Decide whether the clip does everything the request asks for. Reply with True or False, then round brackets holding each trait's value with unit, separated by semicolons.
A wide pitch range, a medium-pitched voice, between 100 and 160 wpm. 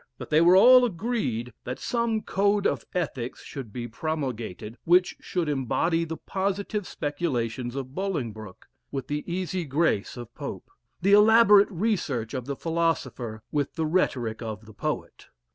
True (7.7 semitones; 155 Hz; 150 wpm)